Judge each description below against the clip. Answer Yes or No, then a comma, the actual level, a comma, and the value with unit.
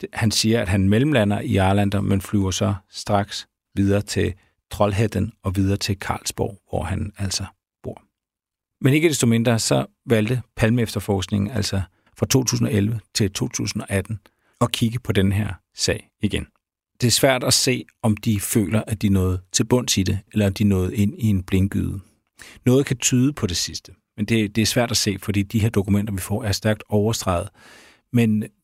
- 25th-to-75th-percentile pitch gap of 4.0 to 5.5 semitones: No, narrow, 2.6 semitones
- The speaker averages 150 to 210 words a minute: Yes, average, 180 wpm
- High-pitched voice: No, low, 105 Hz